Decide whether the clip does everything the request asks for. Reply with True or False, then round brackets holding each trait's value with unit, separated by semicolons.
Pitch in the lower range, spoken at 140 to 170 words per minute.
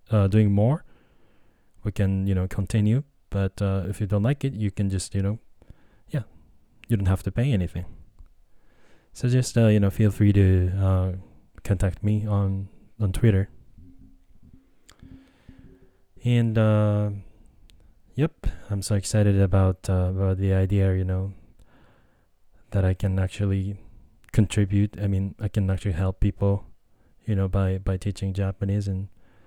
True (100 Hz; 150 wpm)